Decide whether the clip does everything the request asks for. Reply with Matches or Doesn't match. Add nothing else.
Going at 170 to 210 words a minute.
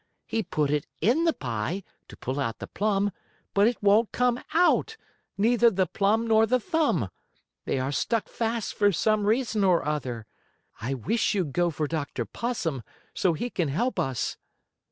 Matches